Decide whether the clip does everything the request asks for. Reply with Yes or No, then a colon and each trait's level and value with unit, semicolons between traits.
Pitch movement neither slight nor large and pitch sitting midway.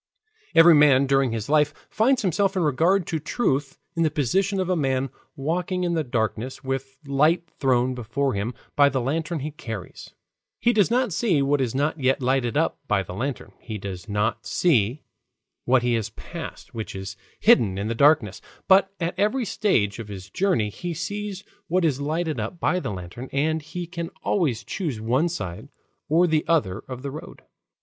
No: wide, 6.1 semitones; medium, 145 Hz